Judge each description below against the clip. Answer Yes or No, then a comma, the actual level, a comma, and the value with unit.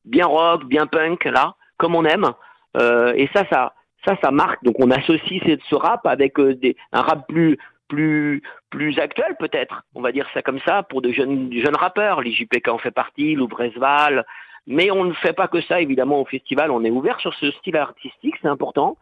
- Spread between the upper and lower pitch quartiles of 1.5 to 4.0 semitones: No, average, 4.5 semitones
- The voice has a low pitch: No, medium, 150 Hz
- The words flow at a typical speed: Yes, average, 205 wpm